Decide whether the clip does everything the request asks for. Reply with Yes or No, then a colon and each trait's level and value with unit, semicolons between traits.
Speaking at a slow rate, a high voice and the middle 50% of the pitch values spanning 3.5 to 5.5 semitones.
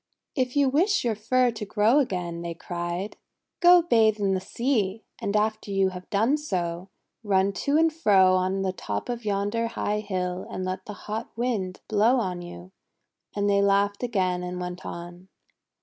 No: average, 180 wpm; high, 200 Hz; average, 3.8 semitones